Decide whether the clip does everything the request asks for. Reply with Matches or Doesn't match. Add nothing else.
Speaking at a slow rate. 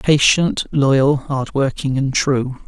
Matches